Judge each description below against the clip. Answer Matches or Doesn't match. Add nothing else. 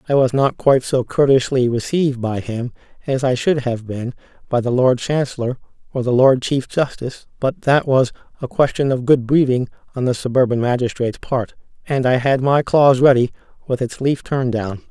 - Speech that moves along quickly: Doesn't match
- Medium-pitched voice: Doesn't match